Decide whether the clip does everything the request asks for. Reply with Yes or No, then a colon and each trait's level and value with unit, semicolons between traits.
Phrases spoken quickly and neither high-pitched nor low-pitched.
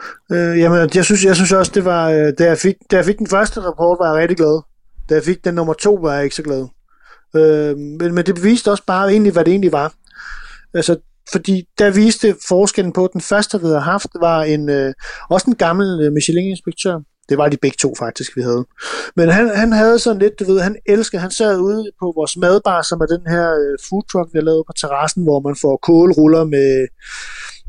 Yes: fast, 225 wpm; medium, 175 Hz